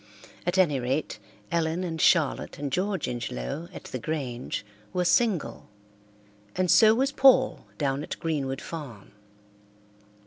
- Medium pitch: Yes, medium, 160 Hz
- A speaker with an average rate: No, slow, 130 wpm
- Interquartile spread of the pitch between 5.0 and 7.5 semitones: Yes, wide, 5.6 semitones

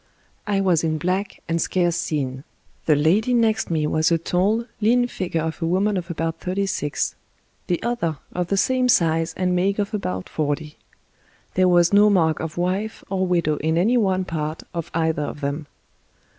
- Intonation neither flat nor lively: Yes, average, 3.7 semitones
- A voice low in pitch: No, medium, 175 Hz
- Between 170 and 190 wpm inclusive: Yes, average, 185 wpm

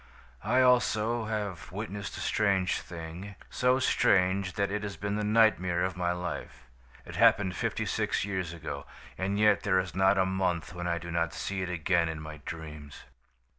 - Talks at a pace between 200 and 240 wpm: No, average, 180 wpm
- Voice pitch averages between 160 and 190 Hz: No, very low, 95 Hz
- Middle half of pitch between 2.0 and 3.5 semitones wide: Yes, average, 3.0 semitones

